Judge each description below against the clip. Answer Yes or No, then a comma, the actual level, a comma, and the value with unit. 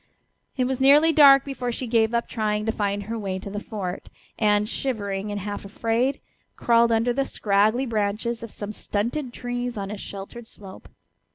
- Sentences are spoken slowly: No, average, 180 wpm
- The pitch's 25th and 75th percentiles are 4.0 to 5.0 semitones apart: No, average, 3.0 semitones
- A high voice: Yes, high, 225 Hz